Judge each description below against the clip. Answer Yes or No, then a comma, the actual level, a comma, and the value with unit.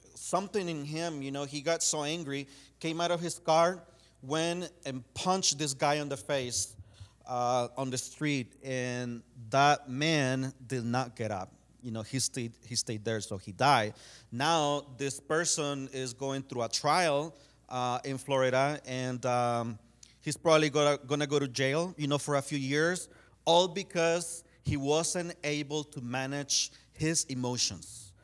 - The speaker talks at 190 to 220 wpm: No, average, 165 wpm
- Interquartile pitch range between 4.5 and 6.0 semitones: No, average, 3.7 semitones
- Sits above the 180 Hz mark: No, medium, 140 Hz